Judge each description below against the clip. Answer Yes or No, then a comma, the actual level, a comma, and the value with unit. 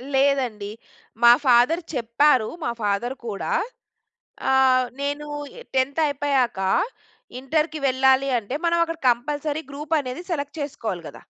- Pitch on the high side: Yes, very high, 265 Hz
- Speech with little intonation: No, average, 3.1 semitones